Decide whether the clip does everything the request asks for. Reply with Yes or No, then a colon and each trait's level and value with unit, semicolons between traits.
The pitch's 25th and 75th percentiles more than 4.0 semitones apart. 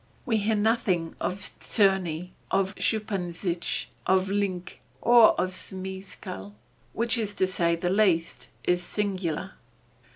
No: average, 2.8 semitones